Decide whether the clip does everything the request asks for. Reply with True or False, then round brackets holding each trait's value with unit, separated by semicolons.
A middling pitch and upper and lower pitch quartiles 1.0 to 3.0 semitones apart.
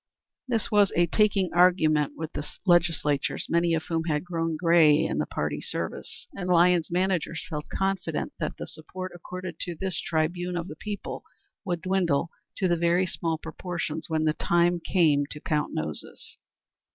True (170 Hz; 2.5 semitones)